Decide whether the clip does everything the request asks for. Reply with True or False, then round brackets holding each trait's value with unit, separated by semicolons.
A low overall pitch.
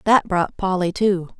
False (190 Hz)